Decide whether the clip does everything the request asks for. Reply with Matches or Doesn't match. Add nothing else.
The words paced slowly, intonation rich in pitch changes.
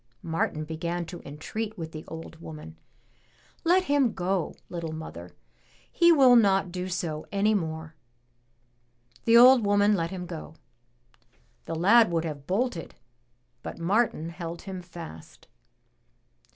Doesn't match